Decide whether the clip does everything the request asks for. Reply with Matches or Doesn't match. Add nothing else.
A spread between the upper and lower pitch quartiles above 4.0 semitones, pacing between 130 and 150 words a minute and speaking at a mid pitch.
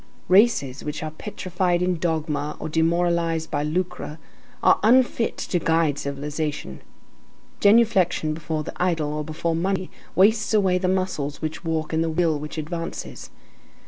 Doesn't match